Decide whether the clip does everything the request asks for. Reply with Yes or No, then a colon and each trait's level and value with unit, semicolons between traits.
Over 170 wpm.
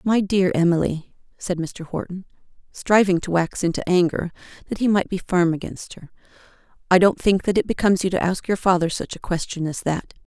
Yes: average, 200 wpm